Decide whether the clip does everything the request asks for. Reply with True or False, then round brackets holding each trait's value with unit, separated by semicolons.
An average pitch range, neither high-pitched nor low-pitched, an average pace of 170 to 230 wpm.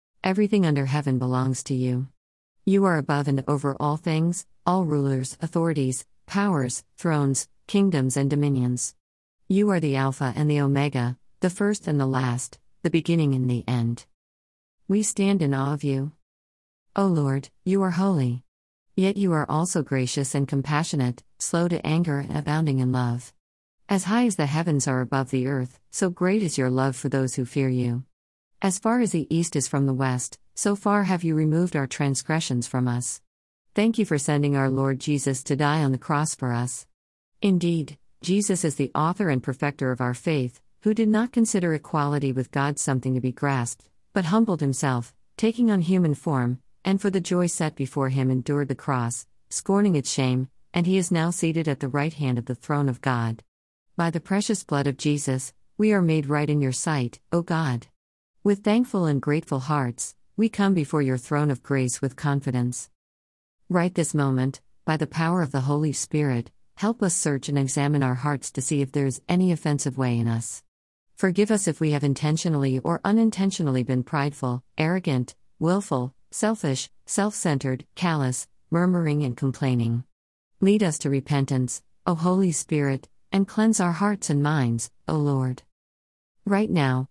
True (4.9 semitones; 145 Hz; 180 wpm)